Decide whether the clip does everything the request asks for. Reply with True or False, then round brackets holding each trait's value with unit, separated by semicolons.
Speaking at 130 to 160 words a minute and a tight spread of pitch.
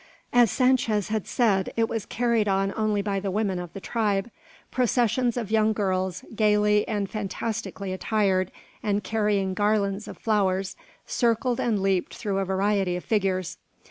True (155 wpm; 2.3 semitones)